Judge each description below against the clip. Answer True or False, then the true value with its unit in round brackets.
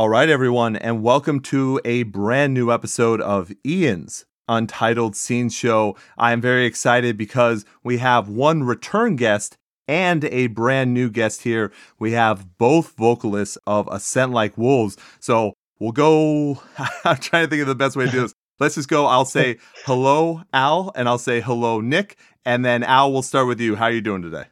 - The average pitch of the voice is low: True (120 Hz)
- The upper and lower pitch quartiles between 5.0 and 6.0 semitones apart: False (3.2 semitones)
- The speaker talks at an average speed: True (190 wpm)